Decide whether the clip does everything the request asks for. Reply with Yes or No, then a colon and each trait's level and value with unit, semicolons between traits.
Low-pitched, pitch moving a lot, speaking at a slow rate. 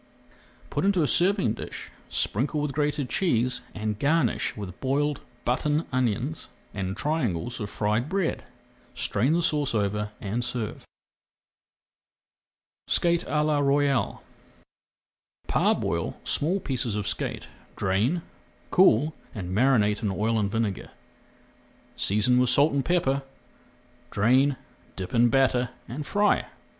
Yes: low, 125 Hz; wide, 5.7 semitones; slow, 120 wpm